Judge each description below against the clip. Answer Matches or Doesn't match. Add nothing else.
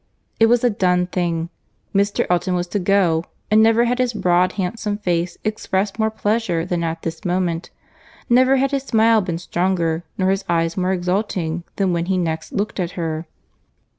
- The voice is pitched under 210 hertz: Matches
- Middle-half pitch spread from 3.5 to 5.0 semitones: Matches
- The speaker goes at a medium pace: Matches